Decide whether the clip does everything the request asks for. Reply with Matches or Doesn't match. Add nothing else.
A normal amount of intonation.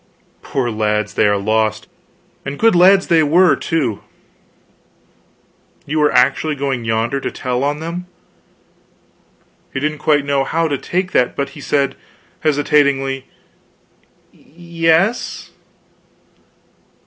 Matches